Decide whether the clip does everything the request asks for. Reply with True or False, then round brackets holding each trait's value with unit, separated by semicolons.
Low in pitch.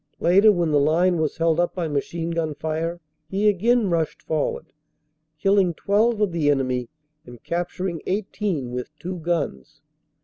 False (170 Hz)